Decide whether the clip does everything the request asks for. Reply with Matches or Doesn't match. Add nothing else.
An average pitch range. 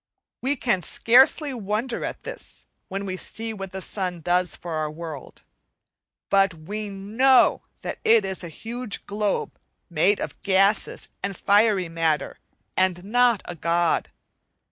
Matches